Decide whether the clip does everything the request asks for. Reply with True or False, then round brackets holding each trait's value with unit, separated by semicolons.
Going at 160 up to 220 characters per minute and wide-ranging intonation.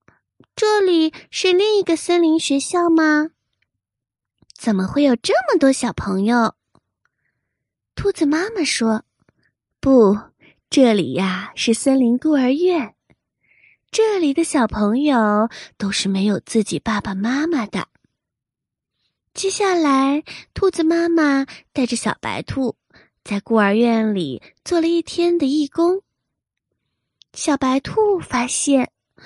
True (170 characters per minute; 7.0 semitones)